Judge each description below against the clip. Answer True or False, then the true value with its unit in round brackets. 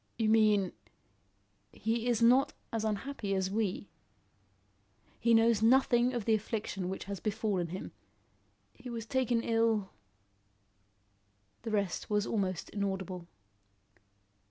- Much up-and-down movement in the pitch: False (3.6 semitones)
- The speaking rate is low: True (125 wpm)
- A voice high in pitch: True (210 Hz)